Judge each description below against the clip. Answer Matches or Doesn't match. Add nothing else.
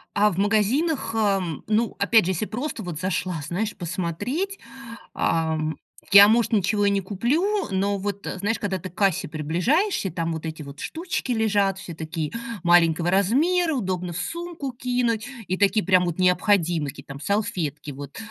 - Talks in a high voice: Matches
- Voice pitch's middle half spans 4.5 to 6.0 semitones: Matches